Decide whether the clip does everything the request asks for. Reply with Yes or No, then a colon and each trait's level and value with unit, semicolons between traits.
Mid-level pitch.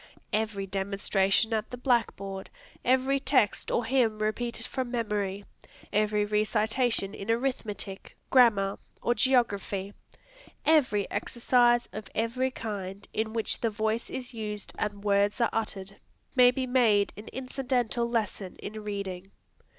No: high, 220 Hz